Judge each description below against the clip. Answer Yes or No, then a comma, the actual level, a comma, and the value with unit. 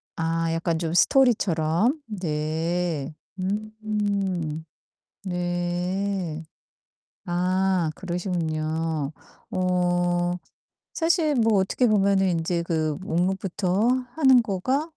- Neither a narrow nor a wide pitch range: Yes, average, 3.5 semitones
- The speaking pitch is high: No, medium, 180 Hz